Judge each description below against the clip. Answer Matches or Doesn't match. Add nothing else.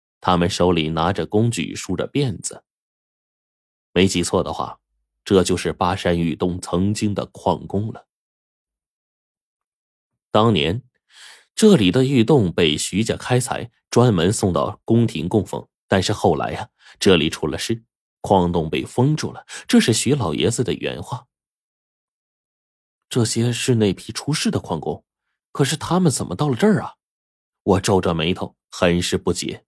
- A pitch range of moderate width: Doesn't match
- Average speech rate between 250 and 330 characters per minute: Doesn't match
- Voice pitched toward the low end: Matches